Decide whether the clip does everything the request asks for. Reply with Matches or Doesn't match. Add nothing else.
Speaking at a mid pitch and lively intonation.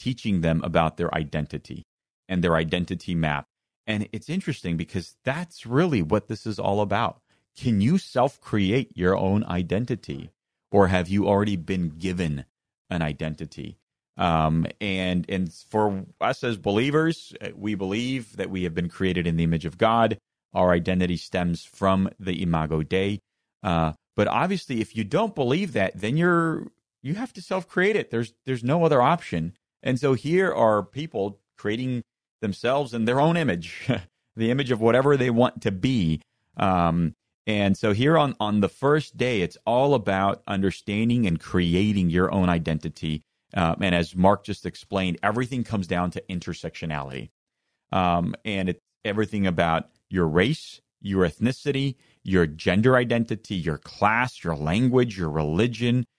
Doesn't match